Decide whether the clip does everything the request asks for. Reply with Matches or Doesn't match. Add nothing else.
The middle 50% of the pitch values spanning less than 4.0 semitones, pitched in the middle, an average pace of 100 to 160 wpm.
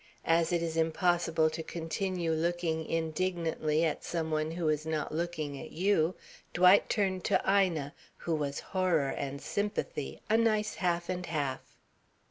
Matches